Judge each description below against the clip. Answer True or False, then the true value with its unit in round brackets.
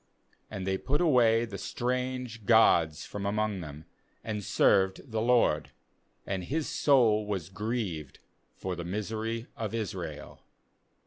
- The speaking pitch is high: False (105 Hz)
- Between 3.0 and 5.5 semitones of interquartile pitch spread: True (3.6 semitones)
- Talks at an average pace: False (130 wpm)